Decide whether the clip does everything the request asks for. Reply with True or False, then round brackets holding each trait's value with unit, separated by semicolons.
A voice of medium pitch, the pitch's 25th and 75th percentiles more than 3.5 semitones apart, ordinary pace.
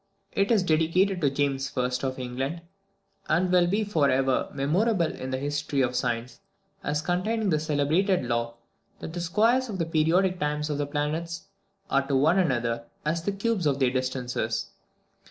True (150 Hz; 5.1 semitones; 170 wpm)